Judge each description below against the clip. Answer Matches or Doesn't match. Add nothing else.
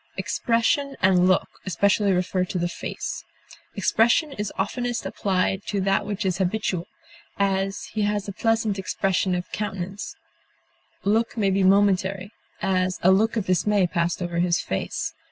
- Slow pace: Doesn't match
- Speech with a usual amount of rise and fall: Doesn't match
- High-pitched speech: Matches